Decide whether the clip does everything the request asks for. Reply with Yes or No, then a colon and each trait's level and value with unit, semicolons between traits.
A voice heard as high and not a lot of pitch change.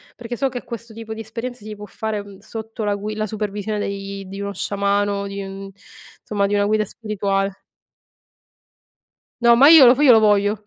Yes: high, 210 Hz; narrow, 1.9 semitones